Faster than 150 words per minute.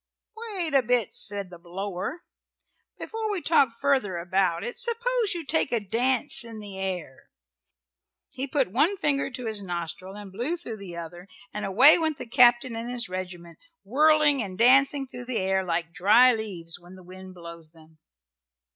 Yes: average, 175 wpm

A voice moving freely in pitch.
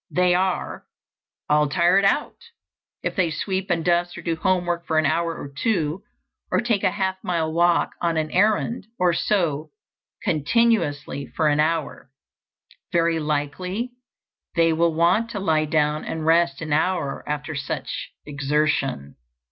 No: average, 3.3 semitones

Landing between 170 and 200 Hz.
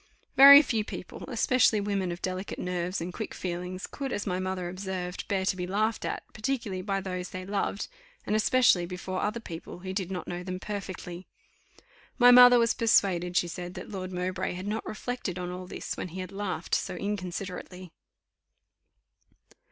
Yes: medium, 185 Hz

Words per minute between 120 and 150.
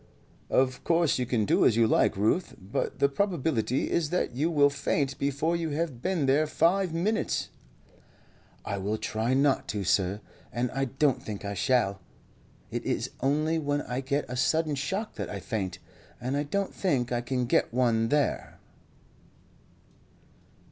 No: average, 165 wpm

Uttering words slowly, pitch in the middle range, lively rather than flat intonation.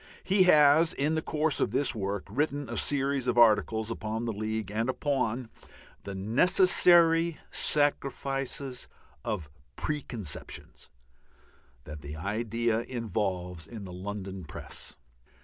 No: slow, 120 wpm; low, 115 Hz; wide, 5.9 semitones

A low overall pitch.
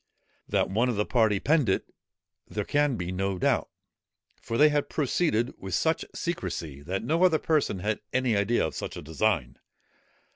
Yes: low, 110 Hz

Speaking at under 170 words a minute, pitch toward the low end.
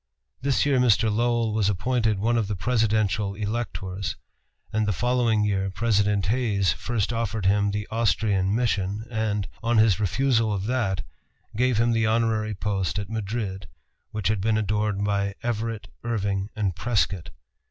Yes: average, 150 wpm; low, 105 Hz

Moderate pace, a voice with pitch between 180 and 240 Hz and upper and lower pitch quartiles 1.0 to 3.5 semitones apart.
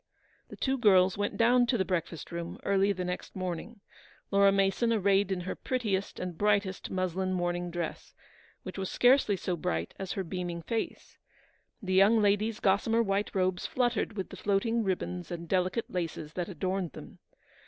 Yes: average, 170 wpm; high, 190 Hz; narrow, 2.5 semitones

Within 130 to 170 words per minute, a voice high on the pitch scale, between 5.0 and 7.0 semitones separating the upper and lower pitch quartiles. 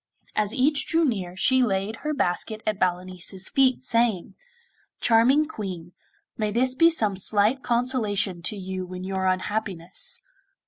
Yes: average, 140 wpm; high, 210 Hz; wide, 5.4 semitones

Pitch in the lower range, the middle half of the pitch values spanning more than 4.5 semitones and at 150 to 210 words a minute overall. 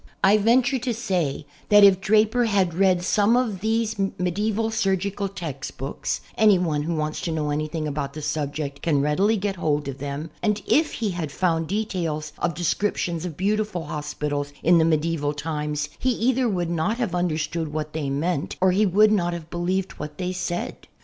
No: medium, 175 Hz; average, 5.2 semitones; average, 195 wpm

